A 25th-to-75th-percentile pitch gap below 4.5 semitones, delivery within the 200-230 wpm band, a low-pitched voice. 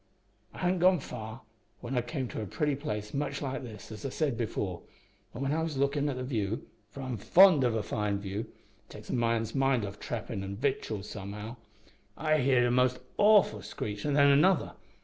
No: average, 4.8 semitones; fast, 205 wpm; low, 125 Hz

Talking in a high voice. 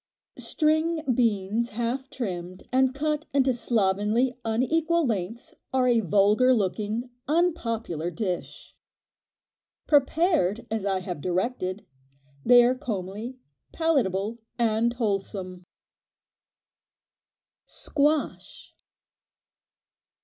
Yes: high, 235 Hz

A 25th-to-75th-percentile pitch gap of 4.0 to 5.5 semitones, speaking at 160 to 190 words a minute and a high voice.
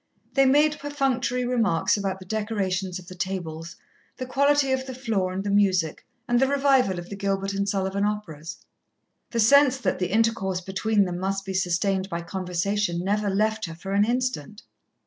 Yes: average, 4.6 semitones; average, 180 wpm; high, 200 Hz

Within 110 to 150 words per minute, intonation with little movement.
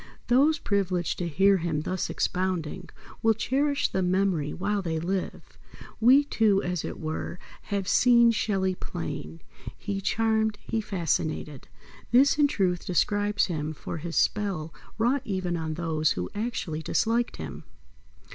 No: average, 140 wpm; average, 4.7 semitones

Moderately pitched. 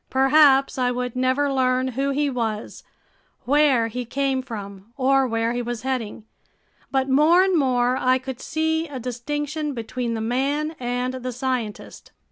No: very high, 255 Hz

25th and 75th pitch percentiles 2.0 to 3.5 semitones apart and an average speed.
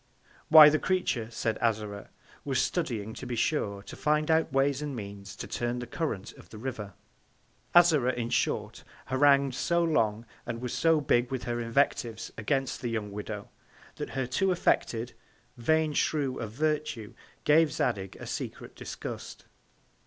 No: average, 5.1 semitones; average, 160 wpm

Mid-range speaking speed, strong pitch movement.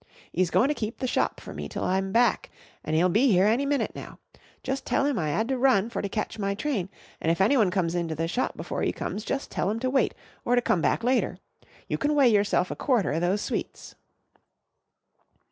No: fast, 230 wpm; wide, 5.8 semitones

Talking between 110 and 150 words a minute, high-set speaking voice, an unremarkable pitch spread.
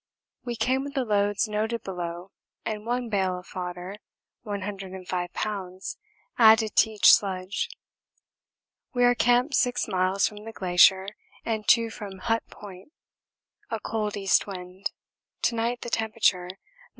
Yes: average, 140 wpm; high, 205 Hz; average, 3.3 semitones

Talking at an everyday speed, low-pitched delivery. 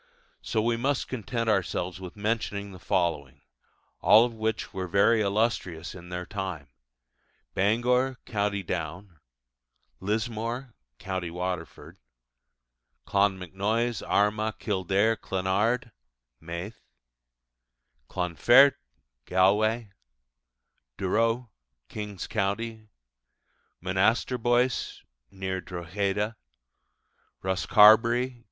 No: slow, 80 wpm; low, 100 Hz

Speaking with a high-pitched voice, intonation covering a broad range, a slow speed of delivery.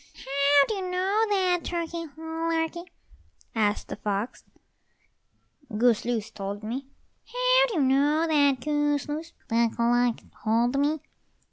Yes: very high, 290 Hz; wide, 5.9 semitones; slow, 130 wpm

